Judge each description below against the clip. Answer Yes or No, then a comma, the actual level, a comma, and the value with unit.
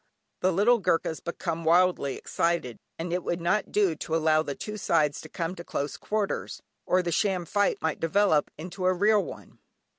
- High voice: No, medium, 175 Hz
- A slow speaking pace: No, average, 185 wpm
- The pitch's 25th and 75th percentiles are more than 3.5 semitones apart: No, average, 3.2 semitones